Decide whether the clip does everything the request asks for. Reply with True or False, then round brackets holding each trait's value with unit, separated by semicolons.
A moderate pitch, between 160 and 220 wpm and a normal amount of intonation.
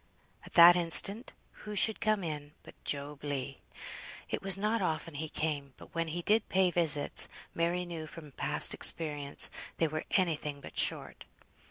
True (165 Hz; 170 wpm; 3.6 semitones)